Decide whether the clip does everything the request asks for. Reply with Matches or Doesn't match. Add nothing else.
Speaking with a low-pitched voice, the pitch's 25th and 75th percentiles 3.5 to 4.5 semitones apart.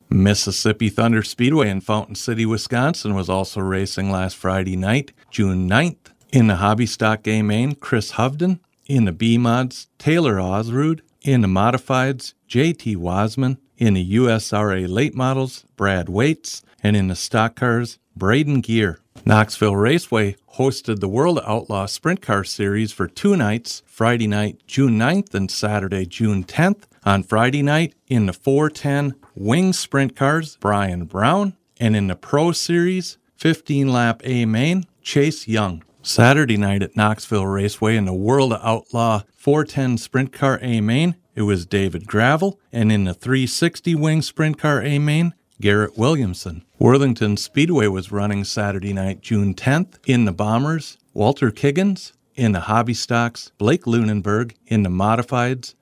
Doesn't match